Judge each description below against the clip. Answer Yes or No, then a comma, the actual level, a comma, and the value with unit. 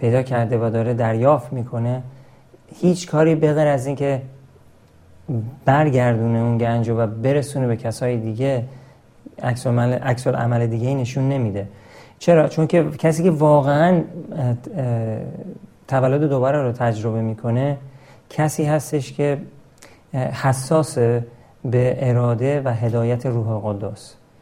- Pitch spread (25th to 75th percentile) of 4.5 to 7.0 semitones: No, average, 3.2 semitones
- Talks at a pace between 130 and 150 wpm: No, average, 120 wpm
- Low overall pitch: Yes, low, 130 Hz